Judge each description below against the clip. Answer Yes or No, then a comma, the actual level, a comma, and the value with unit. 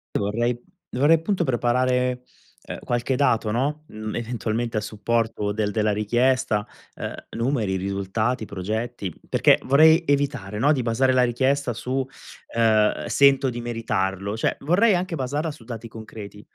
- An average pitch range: Yes, average, 3.7 semitones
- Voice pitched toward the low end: Yes, low, 120 Hz